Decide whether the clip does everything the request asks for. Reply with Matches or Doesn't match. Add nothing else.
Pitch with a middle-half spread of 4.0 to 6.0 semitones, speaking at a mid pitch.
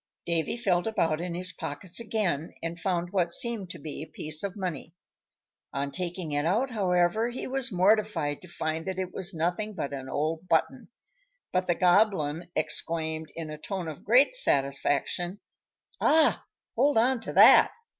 Matches